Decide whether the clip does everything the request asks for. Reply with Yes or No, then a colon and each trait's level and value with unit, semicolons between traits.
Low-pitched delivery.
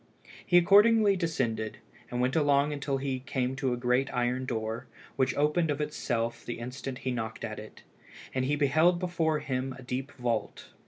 Yes: low, 130 Hz